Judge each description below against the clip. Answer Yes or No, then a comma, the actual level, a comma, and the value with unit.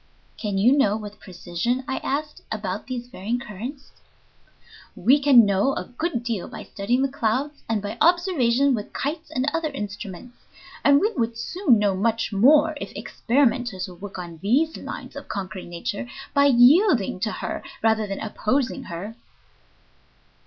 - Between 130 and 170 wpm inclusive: Yes, average, 160 wpm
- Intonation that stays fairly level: No, average, 5.3 semitones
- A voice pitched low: No, high, 240 Hz